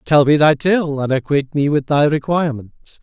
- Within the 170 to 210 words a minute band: Yes, average, 200 wpm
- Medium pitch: Yes, medium, 145 Hz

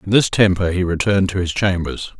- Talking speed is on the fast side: Yes, fast, 220 wpm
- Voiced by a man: Yes, male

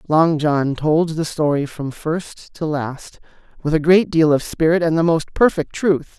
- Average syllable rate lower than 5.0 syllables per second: Yes, 4.1 syllables/s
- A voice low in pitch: No, medium, 155 Hz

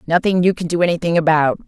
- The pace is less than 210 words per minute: No, fast, 215 wpm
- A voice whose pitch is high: No, medium, 165 Hz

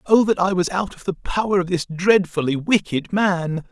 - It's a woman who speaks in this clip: No, male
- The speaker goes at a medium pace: No, fast, 210 wpm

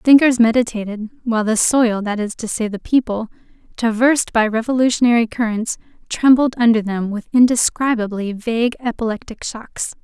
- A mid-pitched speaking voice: No, high, 230 Hz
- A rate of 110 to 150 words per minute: Yes, average, 140 wpm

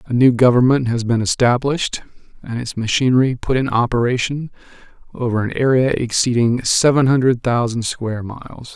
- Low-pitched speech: Yes, low, 125 Hz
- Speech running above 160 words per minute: No, average, 145 wpm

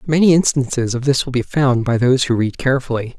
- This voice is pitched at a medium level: No, low, 130 Hz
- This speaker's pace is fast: Yes, fast, 225 wpm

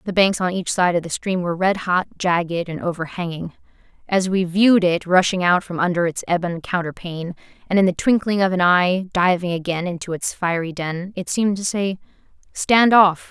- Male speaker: No, female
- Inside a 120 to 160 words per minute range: No, average, 200 wpm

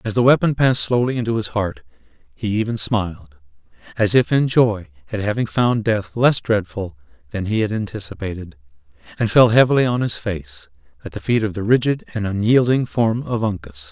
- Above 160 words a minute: Yes, average, 180 wpm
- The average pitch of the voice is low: Yes, low, 105 Hz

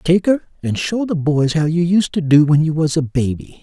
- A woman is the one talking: No, male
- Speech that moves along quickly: Yes, fast, 265 wpm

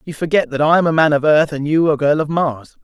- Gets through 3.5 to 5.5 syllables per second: No, 5.9 syllables/s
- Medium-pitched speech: Yes, medium, 155 Hz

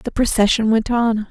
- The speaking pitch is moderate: No, high, 225 Hz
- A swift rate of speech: No, average, 185 wpm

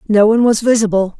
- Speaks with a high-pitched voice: Yes, high, 215 Hz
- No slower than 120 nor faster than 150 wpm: No, average, 200 wpm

